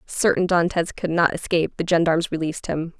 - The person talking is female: Yes, female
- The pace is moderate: Yes, average, 180 wpm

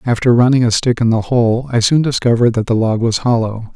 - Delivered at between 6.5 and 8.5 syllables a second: No, 5.8 syllables/s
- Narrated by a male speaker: Yes, male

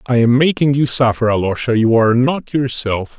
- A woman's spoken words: No, male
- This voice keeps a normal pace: Yes, average, 190 wpm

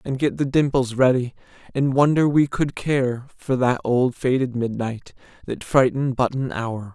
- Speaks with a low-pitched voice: Yes, low, 130 Hz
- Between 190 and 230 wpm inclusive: No, average, 175 wpm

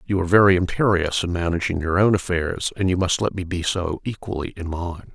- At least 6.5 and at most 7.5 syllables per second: No, 5.8 syllables/s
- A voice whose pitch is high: No, very low, 90 Hz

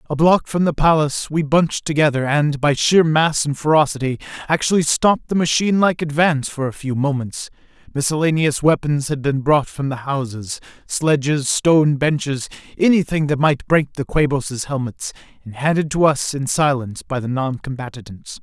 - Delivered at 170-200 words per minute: No, average, 155 wpm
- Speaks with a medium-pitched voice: Yes, medium, 145 Hz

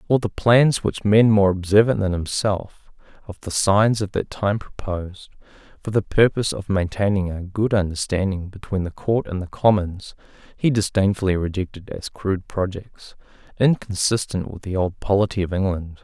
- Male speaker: Yes, male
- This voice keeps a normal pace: Yes, average, 160 wpm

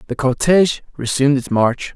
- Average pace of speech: Yes, average, 155 wpm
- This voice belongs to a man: Yes, male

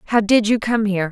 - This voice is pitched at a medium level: No, high, 215 Hz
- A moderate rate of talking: No, fast, 270 wpm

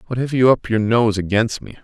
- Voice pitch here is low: Yes, low, 115 Hz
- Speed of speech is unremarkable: No, fast, 260 wpm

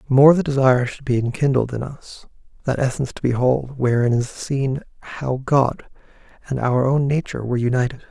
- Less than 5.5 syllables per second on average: No, 5.6 syllables/s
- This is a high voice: No, low, 130 Hz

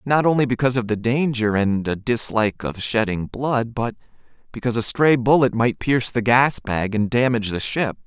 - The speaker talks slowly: No, average, 195 wpm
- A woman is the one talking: No, male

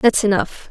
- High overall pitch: Yes, high, 210 Hz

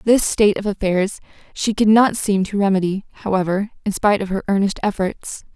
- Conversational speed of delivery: Yes, average, 185 wpm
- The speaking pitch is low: No, high, 200 Hz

